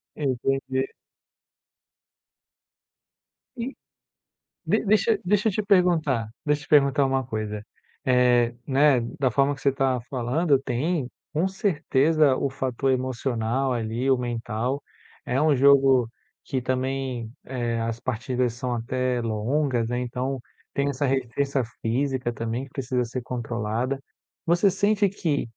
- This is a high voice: No, low, 130 Hz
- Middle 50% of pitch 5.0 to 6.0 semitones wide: No, average, 2.8 semitones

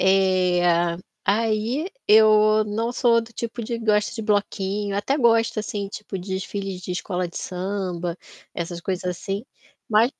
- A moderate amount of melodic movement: Yes, average, 3.0 semitones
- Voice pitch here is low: No, high, 205 Hz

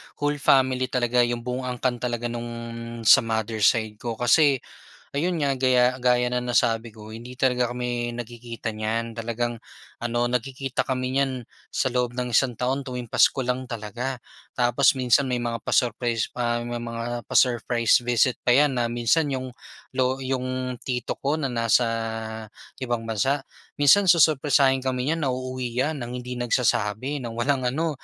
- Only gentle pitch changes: Yes, narrow, 1.8 semitones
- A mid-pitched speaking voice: No, low, 125 Hz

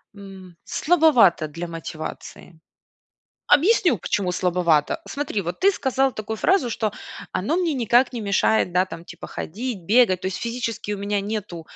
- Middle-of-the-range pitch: No, high, 205 Hz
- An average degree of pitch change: No, wide, 5.8 semitones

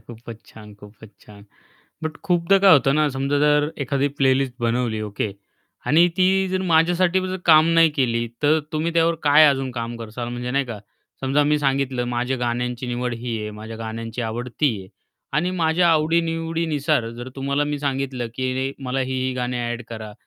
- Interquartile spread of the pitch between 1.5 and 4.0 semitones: No, average, 4.4 semitones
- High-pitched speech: No, low, 135 Hz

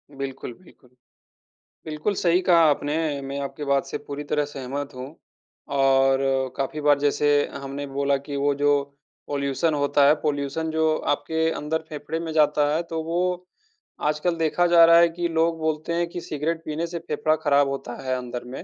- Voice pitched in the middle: Yes, medium, 150 Hz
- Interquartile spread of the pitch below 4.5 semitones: Yes, narrow, 2.6 semitones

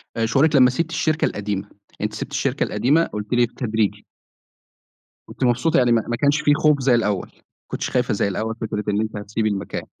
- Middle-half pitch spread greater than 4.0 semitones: Yes, average, 4.6 semitones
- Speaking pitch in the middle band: No, low, 120 Hz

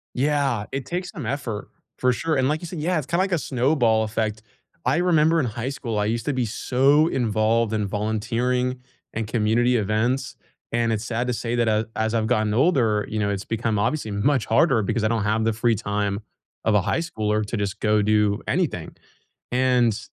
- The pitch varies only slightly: No, average, 3.5 semitones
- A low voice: Yes, low, 115 Hz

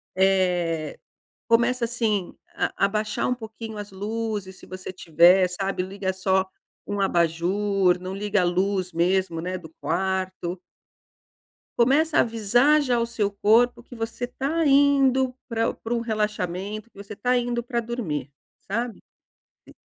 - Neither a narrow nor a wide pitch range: Yes, average, 4.1 semitones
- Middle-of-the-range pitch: No, high, 205 Hz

